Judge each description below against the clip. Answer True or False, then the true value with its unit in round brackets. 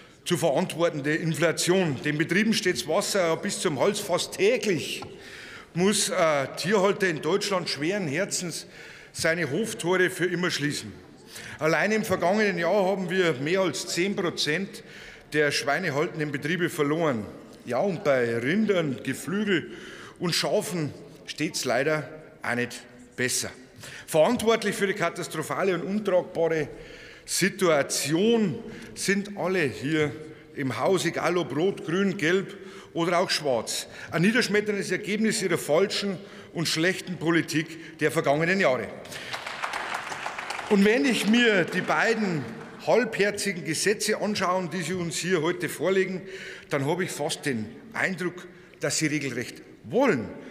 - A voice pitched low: False (175 Hz)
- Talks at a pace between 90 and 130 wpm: True (125 wpm)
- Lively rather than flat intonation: False (4.0 semitones)